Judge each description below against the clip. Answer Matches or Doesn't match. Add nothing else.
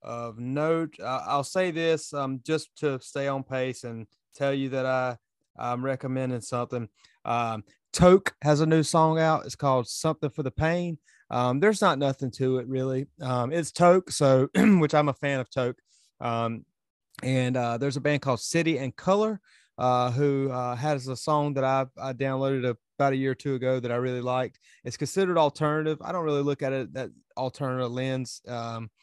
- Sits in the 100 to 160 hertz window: Matches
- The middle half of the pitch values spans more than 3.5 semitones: Doesn't match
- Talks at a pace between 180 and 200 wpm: Matches